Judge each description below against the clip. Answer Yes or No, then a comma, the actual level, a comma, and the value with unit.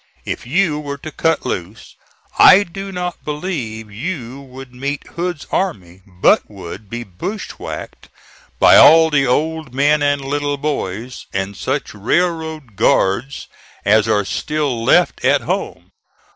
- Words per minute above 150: No, slow, 135 wpm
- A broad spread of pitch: Yes, wide, 6.4 semitones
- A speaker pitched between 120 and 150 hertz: Yes, medium, 140 Hz